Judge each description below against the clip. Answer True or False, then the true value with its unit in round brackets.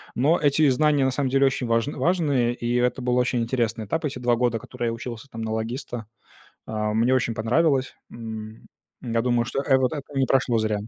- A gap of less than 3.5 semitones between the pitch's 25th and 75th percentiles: True (2.8 semitones)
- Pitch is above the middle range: False (125 Hz)